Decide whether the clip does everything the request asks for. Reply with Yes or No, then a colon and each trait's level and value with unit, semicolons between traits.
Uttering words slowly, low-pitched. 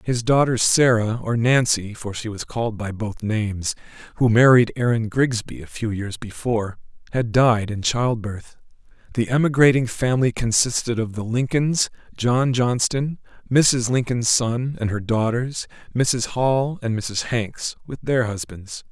No: average, 150 wpm; low, 115 Hz